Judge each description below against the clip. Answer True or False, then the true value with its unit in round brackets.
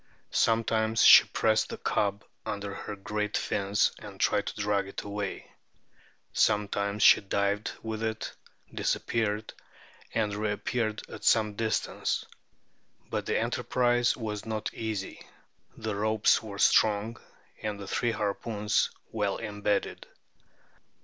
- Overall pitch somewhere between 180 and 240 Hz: False (105 Hz)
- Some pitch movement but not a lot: False (1.4 semitones)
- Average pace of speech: False (125 wpm)